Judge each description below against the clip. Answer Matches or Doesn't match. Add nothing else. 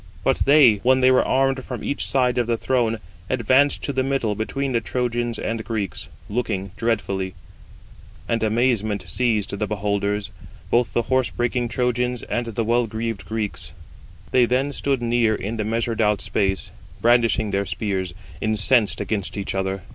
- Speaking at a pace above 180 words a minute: Doesn't match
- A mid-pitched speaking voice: Doesn't match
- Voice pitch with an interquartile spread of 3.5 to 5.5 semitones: Doesn't match